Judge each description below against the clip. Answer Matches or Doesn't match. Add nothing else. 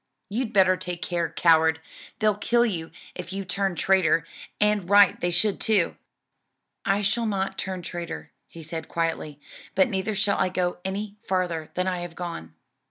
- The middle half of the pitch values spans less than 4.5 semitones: Matches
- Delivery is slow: Doesn't match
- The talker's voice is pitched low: Doesn't match